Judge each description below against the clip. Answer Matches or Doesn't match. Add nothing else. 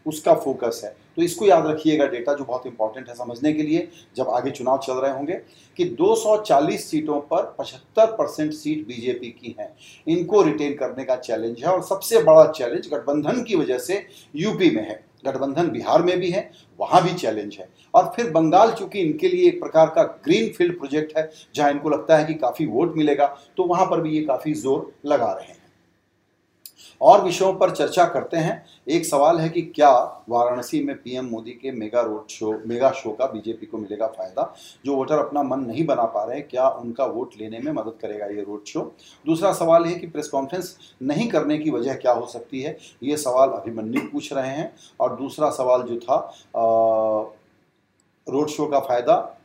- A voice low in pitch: Doesn't match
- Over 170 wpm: Matches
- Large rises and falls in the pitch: Matches